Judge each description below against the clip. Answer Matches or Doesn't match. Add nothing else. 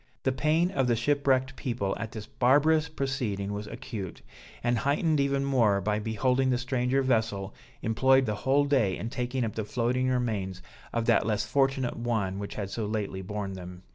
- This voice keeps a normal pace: Matches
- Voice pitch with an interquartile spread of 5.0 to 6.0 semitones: Doesn't match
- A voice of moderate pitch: Doesn't match